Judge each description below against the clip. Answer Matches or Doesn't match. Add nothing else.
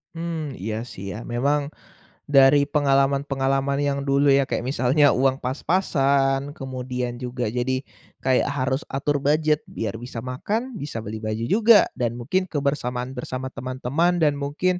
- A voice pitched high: Doesn't match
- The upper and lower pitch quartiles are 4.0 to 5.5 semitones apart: Doesn't match